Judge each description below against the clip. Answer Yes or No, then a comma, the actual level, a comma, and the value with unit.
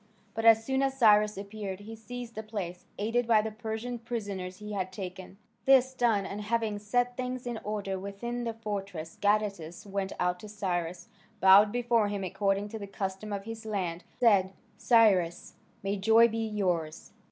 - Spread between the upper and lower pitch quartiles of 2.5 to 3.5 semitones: Yes, average, 2.8 semitones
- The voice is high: Yes, high, 210 Hz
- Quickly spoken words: No, average, 175 wpm